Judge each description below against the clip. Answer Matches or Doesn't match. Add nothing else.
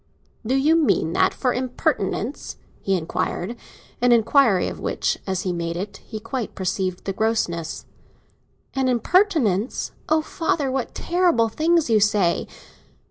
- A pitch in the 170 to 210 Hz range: Doesn't match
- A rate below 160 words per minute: Matches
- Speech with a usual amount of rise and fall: Doesn't match